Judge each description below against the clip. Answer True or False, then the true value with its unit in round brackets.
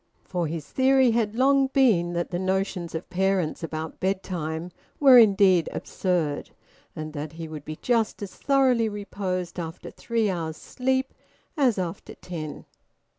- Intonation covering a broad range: True (5.9 semitones)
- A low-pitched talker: False (185 Hz)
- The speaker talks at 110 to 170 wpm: True (145 wpm)